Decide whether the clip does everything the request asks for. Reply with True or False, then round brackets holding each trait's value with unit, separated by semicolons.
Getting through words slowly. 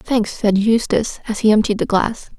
False (200 wpm)